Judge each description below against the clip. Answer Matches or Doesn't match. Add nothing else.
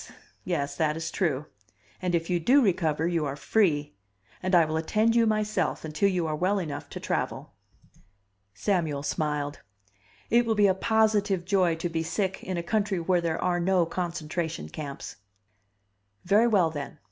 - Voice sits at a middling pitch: Matches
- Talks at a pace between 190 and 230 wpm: Doesn't match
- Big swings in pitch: Doesn't match